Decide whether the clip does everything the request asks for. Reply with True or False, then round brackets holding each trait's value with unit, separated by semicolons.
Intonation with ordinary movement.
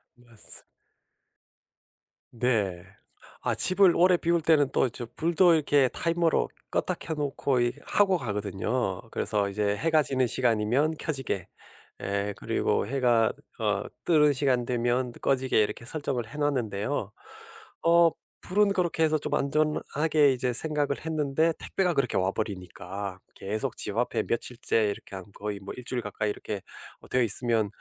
False (6.3 semitones)